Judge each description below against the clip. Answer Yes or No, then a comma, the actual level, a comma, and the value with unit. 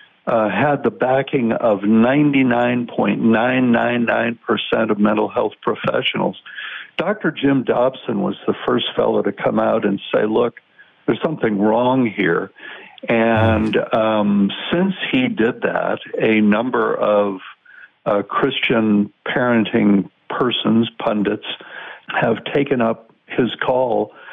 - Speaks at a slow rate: Yes, slow, 115 wpm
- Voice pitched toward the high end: No, low, 115 Hz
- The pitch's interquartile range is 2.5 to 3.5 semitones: Yes, average, 3.2 semitones